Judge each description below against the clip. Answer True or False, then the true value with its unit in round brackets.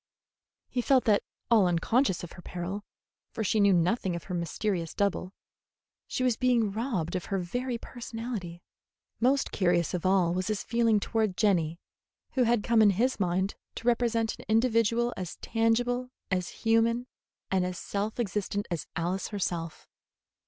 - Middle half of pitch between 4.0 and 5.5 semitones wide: True (4.4 semitones)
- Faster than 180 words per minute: False (160 wpm)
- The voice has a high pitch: True (205 Hz)